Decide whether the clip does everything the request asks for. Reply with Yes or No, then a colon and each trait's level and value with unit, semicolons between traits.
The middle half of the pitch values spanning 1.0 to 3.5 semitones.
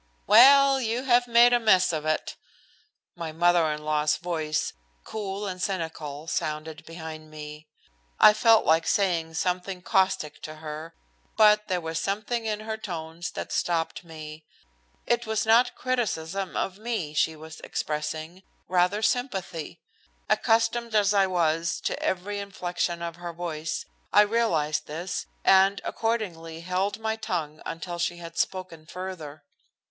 No: average, 4.7 semitones